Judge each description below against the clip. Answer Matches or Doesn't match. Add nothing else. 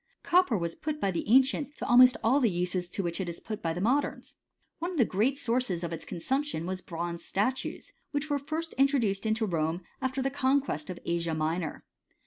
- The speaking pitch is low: Doesn't match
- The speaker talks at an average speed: Doesn't match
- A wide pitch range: Matches